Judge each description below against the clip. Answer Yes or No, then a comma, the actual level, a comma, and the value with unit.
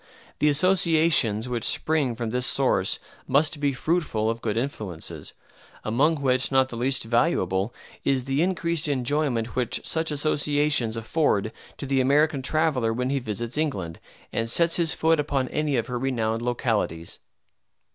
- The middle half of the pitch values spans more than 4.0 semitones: Yes, average, 4.8 semitones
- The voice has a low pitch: Yes, low, 130 Hz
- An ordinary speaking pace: Yes, average, 150 wpm